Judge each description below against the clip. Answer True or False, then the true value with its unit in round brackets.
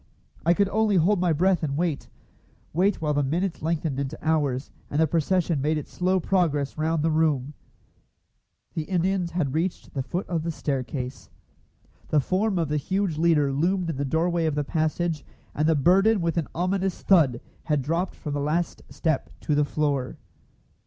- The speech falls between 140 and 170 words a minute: False (180 wpm)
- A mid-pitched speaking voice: True (160 Hz)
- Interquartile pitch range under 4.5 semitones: True (3.3 semitones)